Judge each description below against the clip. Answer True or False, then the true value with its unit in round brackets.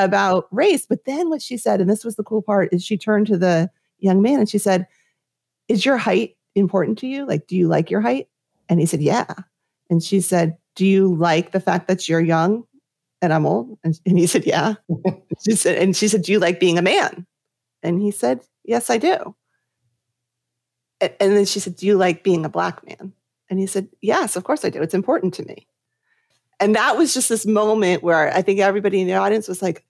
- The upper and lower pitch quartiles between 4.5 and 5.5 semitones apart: False (3.5 semitones)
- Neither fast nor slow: False (230 wpm)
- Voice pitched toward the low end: False (190 Hz)